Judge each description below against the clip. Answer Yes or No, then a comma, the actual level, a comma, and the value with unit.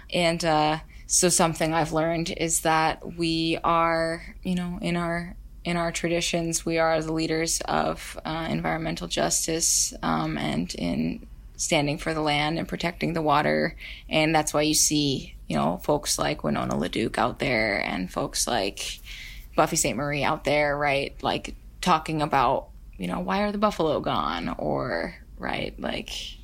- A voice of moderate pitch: Yes, medium, 160 Hz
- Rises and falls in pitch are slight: Yes, narrow, 2.3 semitones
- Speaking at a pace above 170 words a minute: No, average, 160 wpm